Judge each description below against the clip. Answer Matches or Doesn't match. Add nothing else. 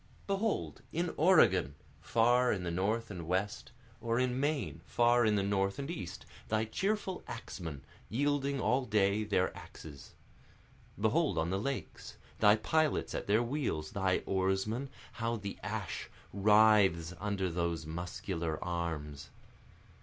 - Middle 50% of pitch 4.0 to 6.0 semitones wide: Matches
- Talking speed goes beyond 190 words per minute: Doesn't match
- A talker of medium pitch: Doesn't match